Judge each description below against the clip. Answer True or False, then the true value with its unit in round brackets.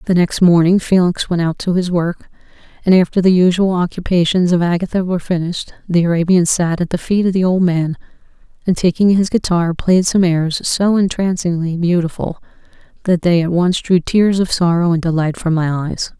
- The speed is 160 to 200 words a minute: True (190 wpm)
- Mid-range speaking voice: True (175 Hz)